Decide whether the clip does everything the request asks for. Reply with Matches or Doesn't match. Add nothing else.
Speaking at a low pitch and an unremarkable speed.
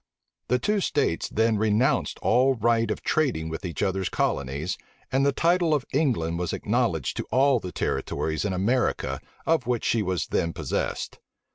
Matches